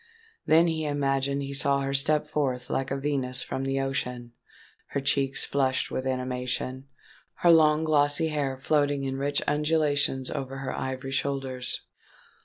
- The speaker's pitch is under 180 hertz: Yes, low, 135 Hz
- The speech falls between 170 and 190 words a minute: No, average, 140 wpm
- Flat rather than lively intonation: Yes, narrow, 1.6 semitones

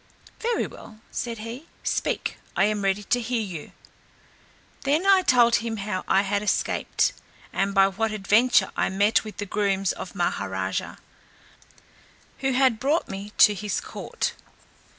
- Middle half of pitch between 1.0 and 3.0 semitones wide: No, average, 3.7 semitones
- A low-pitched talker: No, high, 215 Hz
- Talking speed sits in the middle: Yes, average, 150 wpm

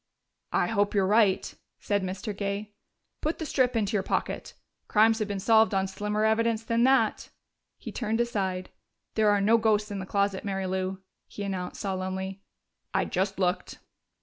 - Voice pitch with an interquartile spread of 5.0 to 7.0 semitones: No, narrow, 2.5 semitones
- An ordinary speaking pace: Yes, average, 170 wpm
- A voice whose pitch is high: Yes, high, 205 Hz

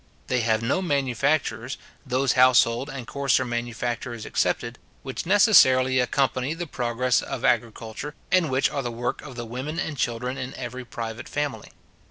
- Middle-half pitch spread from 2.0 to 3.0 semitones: Yes, average, 2.7 semitones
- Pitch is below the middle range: Yes, low, 125 Hz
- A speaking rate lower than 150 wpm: No, average, 155 wpm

